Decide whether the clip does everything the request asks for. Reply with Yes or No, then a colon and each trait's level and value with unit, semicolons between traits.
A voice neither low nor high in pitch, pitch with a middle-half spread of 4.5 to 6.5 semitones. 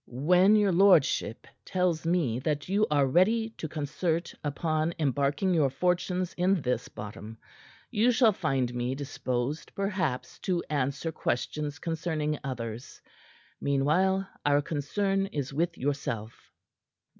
Yes: medium, 155 Hz; average, 5.1 semitones